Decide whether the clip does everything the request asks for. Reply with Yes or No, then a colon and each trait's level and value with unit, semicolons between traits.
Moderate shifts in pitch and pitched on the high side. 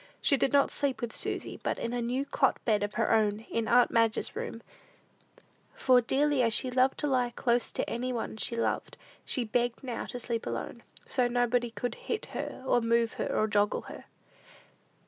No: narrow, 1.9 semitones; high, 240 Hz